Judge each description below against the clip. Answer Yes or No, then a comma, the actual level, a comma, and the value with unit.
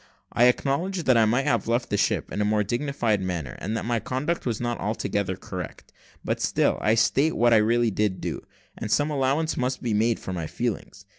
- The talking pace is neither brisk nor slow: No, fast, 215 wpm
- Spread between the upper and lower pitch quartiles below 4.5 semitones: Yes, average, 3.8 semitones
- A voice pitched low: Yes, low, 115 Hz